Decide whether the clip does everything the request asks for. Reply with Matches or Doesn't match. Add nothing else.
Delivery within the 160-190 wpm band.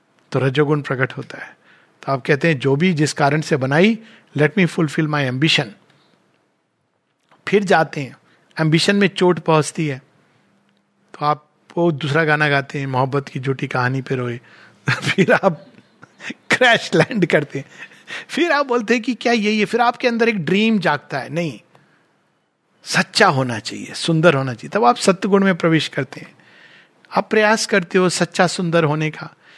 Matches